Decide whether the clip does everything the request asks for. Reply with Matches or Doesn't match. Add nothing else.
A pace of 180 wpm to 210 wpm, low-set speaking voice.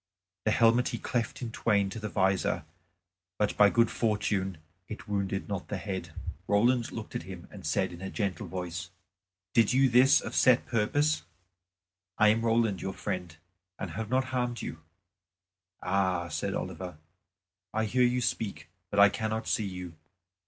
Doesn't match